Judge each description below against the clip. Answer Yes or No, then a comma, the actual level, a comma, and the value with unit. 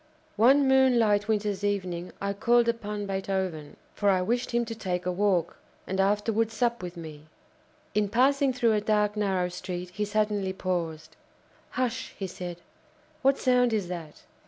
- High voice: Yes, high, 205 Hz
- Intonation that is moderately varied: Yes, average, 4.0 semitones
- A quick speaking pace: No, average, 160 wpm